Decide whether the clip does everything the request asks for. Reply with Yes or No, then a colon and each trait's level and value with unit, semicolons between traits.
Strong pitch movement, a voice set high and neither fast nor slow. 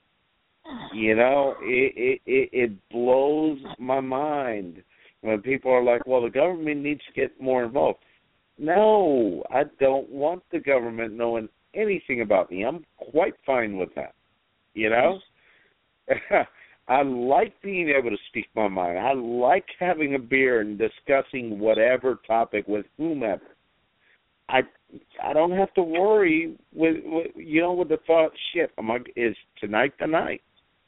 No: wide, 6.1 semitones; low, 135 Hz; average, 145 wpm